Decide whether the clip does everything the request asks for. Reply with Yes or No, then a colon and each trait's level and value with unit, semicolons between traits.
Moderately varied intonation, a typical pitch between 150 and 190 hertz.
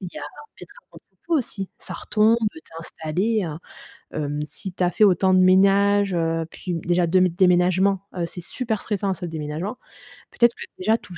Yes: average, 3.0 semitones; medium, 185 Hz